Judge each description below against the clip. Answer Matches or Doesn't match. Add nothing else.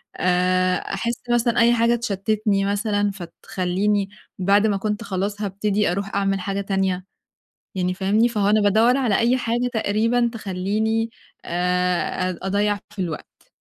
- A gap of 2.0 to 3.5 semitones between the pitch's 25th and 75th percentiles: Matches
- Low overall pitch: Doesn't match